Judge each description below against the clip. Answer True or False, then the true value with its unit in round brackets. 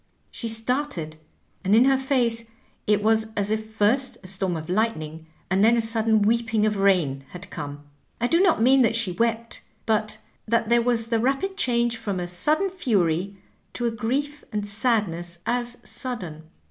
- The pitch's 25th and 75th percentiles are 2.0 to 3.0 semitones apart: False (3.5 semitones)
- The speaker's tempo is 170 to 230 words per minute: True (175 wpm)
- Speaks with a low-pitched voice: False (225 Hz)